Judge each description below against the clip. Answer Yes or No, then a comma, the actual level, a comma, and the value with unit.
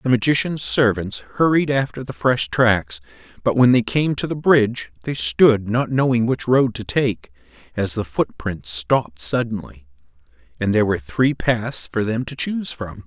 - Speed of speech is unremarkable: Yes, average, 175 wpm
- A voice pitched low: Yes, low, 120 Hz